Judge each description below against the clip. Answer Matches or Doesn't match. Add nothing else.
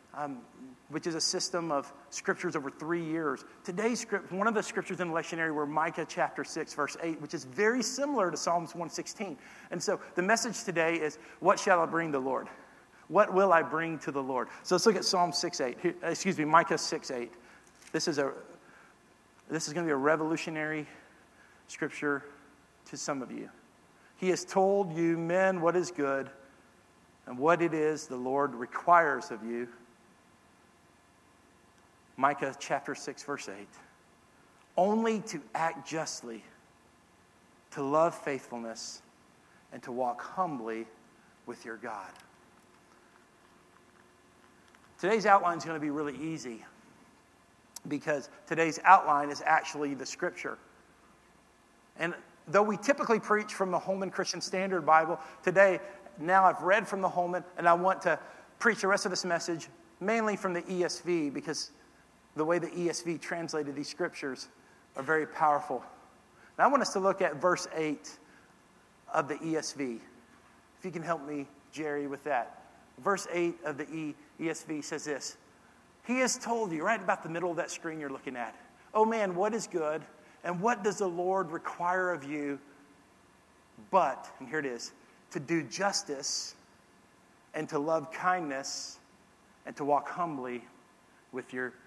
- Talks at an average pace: Matches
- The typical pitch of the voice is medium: Matches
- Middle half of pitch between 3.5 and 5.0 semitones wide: Matches